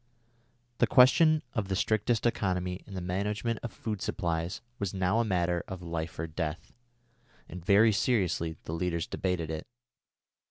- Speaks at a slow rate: No, average, 160 wpm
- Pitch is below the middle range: Yes, very low, 95 Hz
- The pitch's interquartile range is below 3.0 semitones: No, average, 4.0 semitones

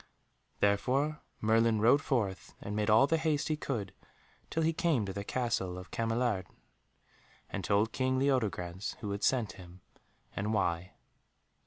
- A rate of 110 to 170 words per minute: Yes, average, 150 wpm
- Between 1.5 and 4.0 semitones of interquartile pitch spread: No, average, 4.6 semitones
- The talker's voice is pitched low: Yes, low, 110 Hz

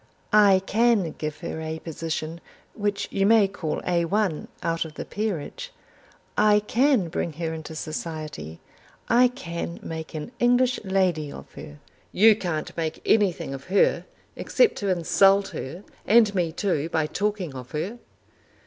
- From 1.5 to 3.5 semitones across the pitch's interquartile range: No, average, 4.6 semitones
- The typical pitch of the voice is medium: Yes, medium, 175 Hz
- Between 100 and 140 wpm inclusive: No, average, 150 wpm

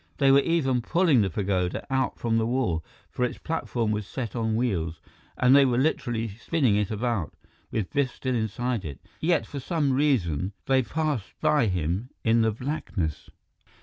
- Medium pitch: No, low, 120 Hz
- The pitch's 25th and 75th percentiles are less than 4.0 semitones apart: No, average, 4.6 semitones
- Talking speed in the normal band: Yes, average, 175 wpm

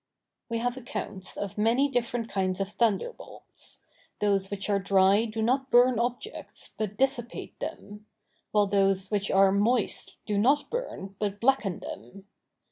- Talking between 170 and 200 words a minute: No, average, 145 wpm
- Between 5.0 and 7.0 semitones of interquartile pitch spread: No, average, 3.6 semitones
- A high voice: Yes, high, 210 Hz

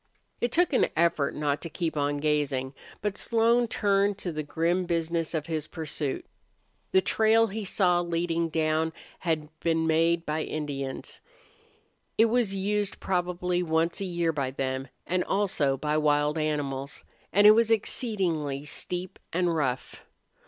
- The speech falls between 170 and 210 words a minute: No, average, 150 wpm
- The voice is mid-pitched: Yes, medium, 165 Hz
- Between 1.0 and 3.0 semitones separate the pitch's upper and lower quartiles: No, average, 4.2 semitones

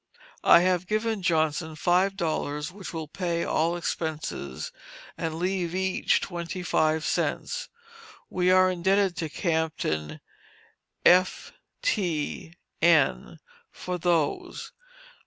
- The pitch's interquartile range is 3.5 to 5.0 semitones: No, average, 2.7 semitones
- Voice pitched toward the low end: No, medium, 175 Hz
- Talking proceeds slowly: Yes, slow, 105 wpm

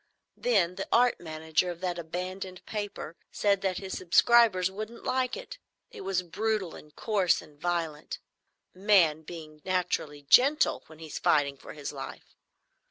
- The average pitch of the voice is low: No, medium, 180 Hz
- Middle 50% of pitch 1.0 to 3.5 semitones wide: No, average, 4.4 semitones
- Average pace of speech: Yes, average, 145 wpm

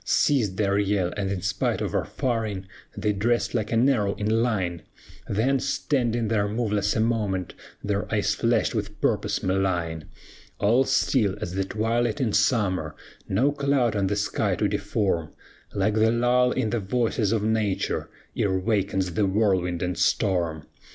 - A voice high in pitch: No, low, 105 Hz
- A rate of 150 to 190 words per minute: Yes, average, 160 wpm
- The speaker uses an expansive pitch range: No, average, 3.3 semitones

